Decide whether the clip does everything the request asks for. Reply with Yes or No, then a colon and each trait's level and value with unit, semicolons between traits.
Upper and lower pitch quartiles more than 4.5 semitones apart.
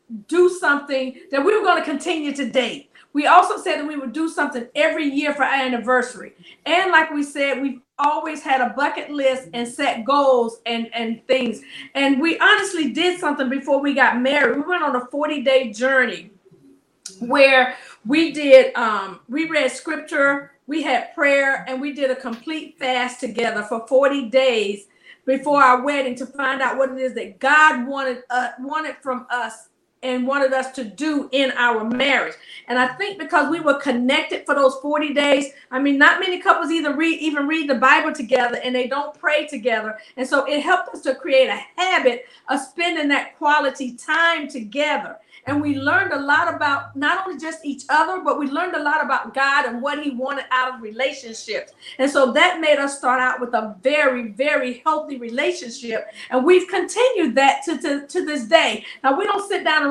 No: average, 3.2 semitones